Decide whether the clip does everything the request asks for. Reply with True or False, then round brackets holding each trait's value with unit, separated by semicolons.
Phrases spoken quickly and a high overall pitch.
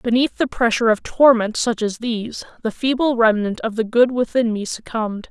False (190 wpm; 230 Hz)